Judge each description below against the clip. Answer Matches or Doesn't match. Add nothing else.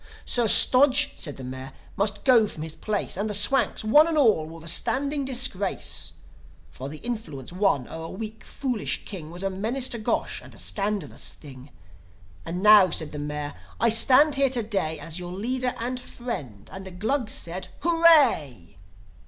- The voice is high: Matches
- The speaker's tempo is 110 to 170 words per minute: Doesn't match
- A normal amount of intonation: Doesn't match